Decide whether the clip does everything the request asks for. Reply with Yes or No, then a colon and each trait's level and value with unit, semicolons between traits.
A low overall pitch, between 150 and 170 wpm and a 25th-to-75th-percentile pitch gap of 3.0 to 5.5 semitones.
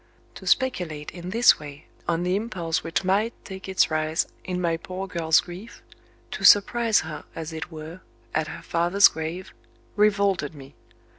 No: medium, 175 Hz; average, 160 wpm; average, 3.6 semitones